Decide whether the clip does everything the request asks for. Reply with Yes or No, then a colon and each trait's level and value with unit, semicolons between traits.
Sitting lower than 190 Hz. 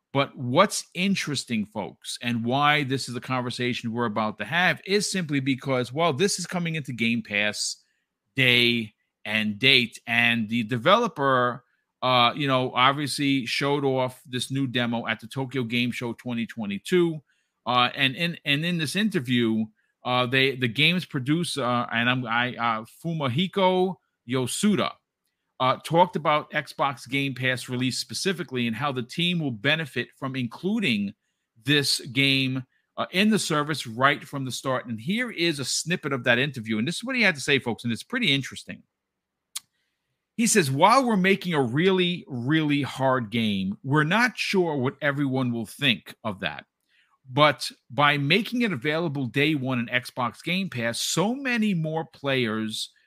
Yes: low, 135 Hz